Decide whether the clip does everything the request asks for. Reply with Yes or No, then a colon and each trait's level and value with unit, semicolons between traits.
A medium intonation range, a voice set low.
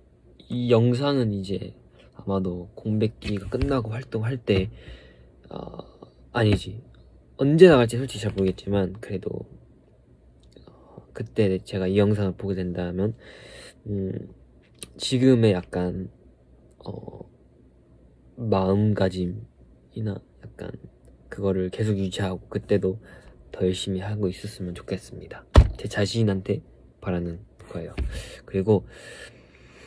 Yes: average, 3.4 semitones; very low, 95 Hz